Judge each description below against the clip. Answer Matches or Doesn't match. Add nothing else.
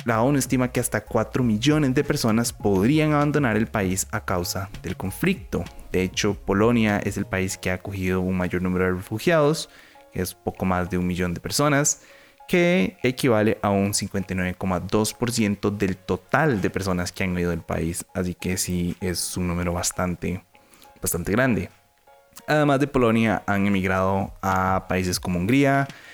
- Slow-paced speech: Doesn't match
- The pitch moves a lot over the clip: Matches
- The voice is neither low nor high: Doesn't match